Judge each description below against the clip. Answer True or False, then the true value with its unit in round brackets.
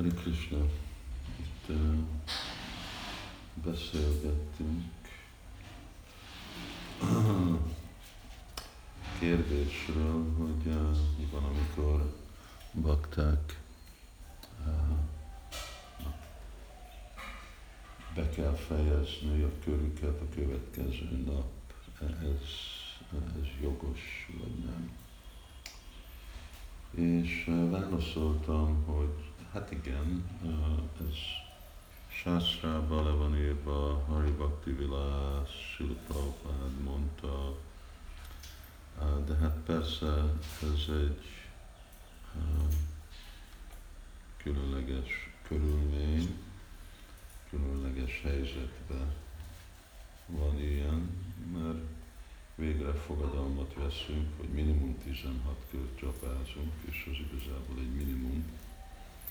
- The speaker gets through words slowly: True (60 wpm)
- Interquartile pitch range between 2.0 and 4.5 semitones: True (2.5 semitones)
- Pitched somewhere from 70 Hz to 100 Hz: True (75 Hz)